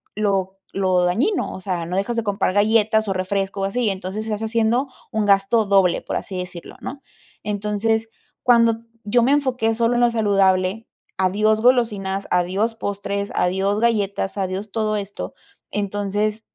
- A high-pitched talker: Yes, high, 205 Hz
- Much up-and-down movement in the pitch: No, narrow, 2.6 semitones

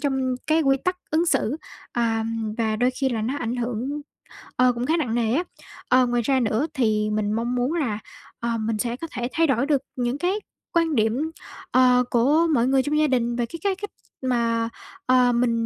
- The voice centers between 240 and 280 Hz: Yes, very high, 250 Hz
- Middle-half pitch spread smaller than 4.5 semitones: Yes, average, 3.6 semitones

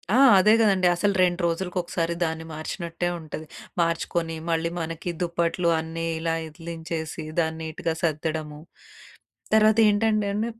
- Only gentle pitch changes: Yes, narrow, 2.3 semitones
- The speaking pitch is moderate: Yes, medium, 170 Hz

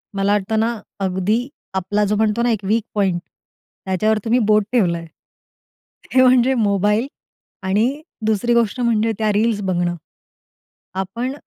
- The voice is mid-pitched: No, high, 215 Hz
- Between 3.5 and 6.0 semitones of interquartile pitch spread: No, average, 3.1 semitones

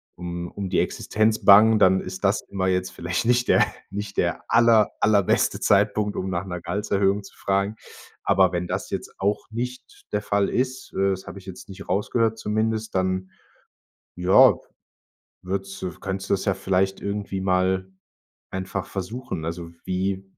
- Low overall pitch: Yes, very low, 95 Hz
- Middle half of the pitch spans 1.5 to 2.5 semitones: Yes, narrow, 2.0 semitones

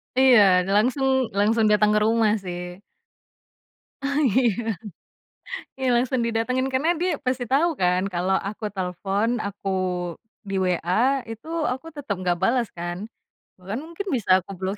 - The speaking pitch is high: Yes, high, 220 Hz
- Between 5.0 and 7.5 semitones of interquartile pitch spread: Yes, average, 5.3 semitones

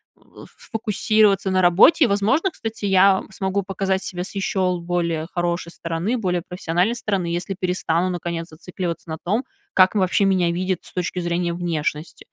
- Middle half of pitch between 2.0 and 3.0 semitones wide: Yes, narrow, 2.4 semitones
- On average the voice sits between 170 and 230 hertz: Yes, medium, 185 Hz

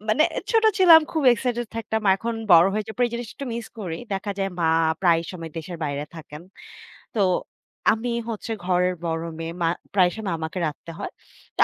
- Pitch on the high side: Yes, high, 195 Hz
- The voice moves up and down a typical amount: No, wide, 5.7 semitones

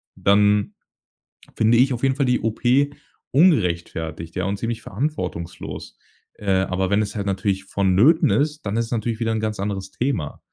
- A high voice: No, low, 105 Hz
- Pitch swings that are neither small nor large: Yes, average, 3.9 semitones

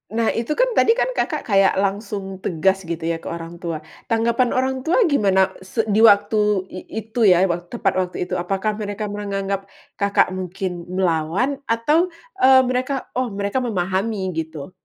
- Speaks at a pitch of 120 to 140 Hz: No, high, 200 Hz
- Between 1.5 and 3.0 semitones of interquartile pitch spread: No, average, 3.7 semitones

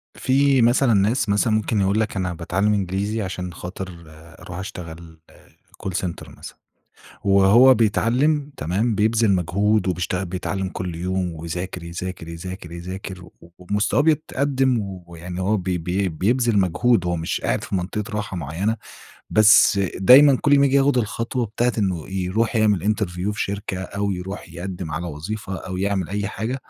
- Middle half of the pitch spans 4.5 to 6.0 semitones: No, average, 3.7 semitones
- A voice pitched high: No, very low, 95 Hz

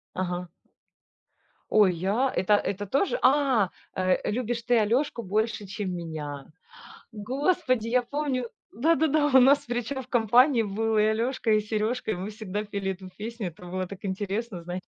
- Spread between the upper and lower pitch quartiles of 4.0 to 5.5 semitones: Yes, average, 4.6 semitones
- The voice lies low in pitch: No, high, 220 Hz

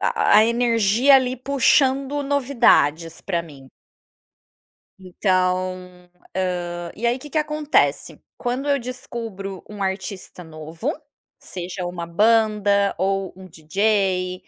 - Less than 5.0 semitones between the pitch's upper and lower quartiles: No, average, 5.3 semitones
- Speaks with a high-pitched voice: Yes, high, 200 Hz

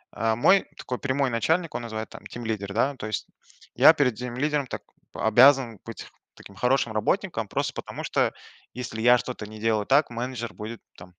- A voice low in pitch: Yes, low, 120 Hz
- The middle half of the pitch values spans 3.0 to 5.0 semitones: Yes, average, 3.4 semitones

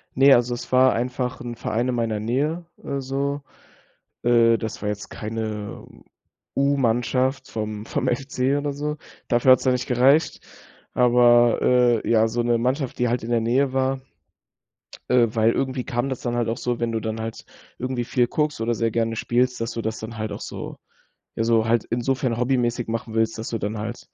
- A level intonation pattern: Yes, narrow, 2.2 semitones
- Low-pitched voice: Yes, low, 120 Hz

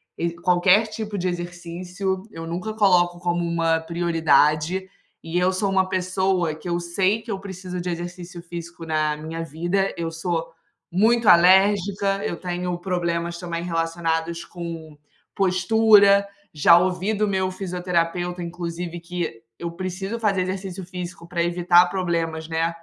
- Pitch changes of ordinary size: No, narrow, 1.9 semitones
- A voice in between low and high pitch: Yes, medium, 175 Hz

